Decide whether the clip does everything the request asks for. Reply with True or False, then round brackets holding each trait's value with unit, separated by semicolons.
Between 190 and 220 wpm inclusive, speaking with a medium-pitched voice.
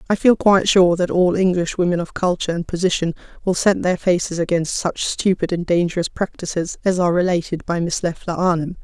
True (195 wpm; 175 Hz)